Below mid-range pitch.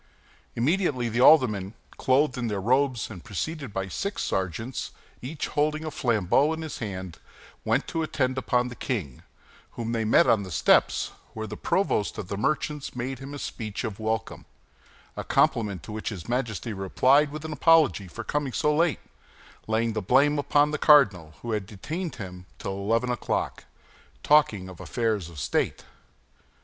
Yes: low, 120 Hz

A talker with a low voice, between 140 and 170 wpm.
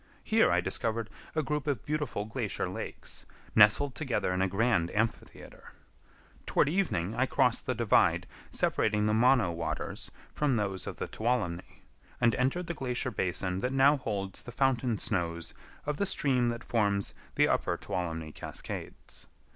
Yes: low, 115 Hz; average, 155 wpm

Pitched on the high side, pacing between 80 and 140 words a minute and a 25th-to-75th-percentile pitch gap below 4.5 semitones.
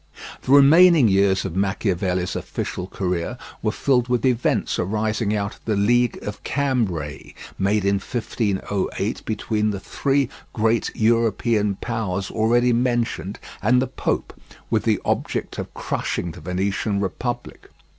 No: low, 105 Hz; slow, 135 wpm; average, 3.9 semitones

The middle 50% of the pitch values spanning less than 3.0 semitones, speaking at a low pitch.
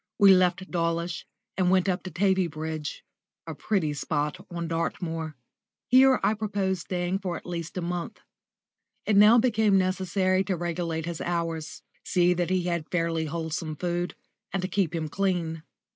No: narrow, 2.4 semitones; medium, 175 Hz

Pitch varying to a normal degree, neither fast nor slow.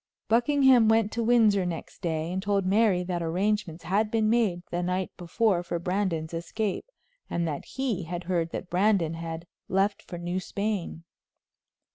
Yes: average, 3.9 semitones; average, 160 wpm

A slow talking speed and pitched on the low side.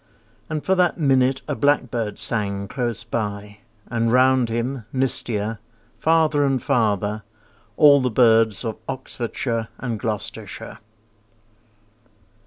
Yes: slow, 110 wpm; low, 120 Hz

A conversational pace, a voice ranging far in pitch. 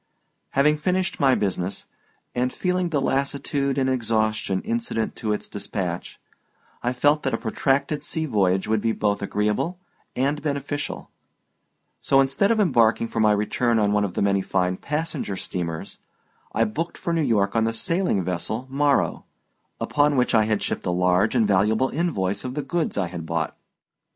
Yes: average, 170 wpm; wide, 6.0 semitones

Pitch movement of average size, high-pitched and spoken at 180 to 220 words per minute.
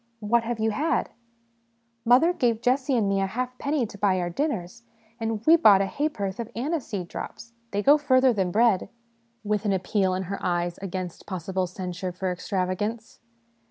Yes: average, 4.0 semitones; high, 220 Hz; average, 190 wpm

